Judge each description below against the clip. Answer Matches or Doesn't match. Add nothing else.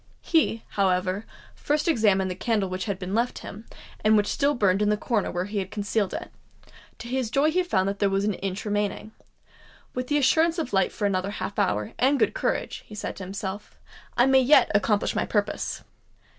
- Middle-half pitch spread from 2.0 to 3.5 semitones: Doesn't match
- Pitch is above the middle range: Matches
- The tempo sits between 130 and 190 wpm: Doesn't match